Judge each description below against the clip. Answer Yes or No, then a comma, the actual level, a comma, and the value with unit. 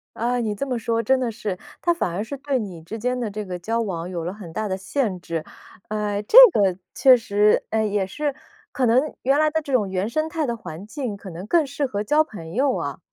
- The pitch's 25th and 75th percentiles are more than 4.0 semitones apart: Yes, average, 5.2 semitones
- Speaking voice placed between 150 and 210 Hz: No, high, 220 Hz